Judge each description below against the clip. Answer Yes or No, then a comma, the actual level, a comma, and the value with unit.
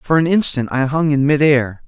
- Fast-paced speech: Yes, fast, 255 wpm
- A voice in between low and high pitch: Yes, medium, 145 Hz